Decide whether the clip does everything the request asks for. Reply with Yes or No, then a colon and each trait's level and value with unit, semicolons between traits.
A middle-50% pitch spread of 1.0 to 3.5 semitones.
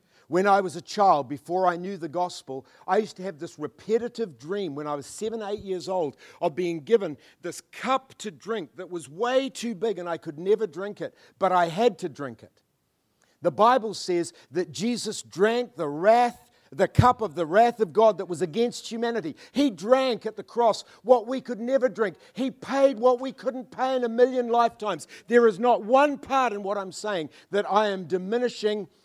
No: average, 4.9 semitones